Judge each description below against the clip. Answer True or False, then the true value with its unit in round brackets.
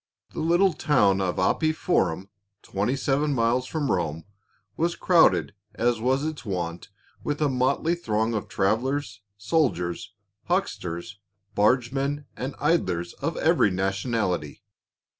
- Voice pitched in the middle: False (120 Hz)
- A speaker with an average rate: False (125 wpm)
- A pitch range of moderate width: False (7.1 semitones)